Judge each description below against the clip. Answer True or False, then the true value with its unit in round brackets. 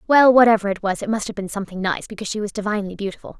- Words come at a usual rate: False (265 wpm)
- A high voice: True (205 Hz)